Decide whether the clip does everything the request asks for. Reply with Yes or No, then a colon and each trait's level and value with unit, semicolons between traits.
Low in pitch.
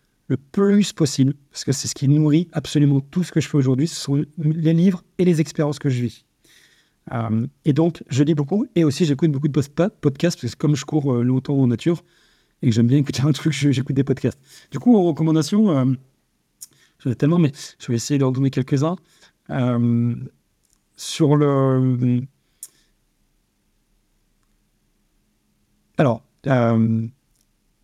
No: medium, 145 Hz